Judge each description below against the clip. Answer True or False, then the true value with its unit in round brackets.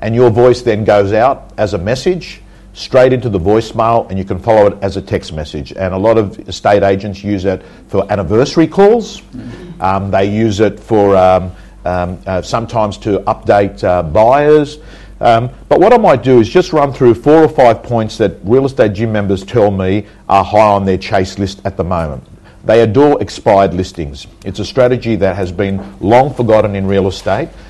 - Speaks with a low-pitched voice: True (105 Hz)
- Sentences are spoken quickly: False (195 wpm)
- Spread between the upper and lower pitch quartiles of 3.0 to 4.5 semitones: True (3.5 semitones)